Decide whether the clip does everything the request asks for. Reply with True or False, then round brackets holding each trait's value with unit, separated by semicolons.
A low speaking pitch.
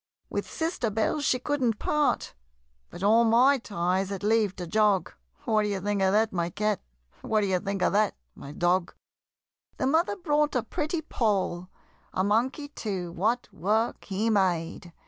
False (210 Hz)